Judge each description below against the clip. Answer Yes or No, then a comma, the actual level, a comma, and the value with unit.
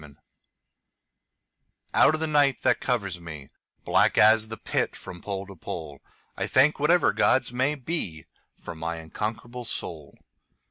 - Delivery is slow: Yes, slow, 130 wpm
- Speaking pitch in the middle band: No, low, 110 Hz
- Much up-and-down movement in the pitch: Yes, wide, 8.0 semitones